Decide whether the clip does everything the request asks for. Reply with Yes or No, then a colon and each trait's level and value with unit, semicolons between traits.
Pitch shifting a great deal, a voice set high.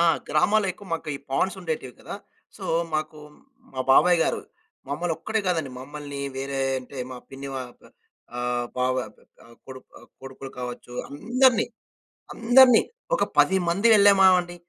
No: wide, 6.6 semitones; medium, 150 Hz